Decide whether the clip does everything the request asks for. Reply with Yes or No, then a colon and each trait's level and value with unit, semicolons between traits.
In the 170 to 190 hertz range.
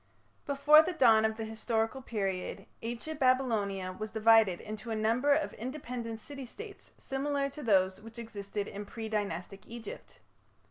No: high, 225 Hz